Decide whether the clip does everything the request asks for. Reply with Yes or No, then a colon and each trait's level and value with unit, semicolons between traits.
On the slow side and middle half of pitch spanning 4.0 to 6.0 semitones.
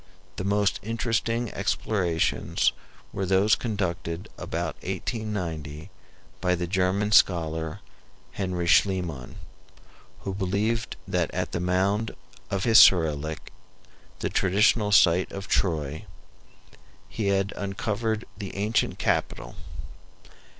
No: slow, 100 wpm; average, 3.3 semitones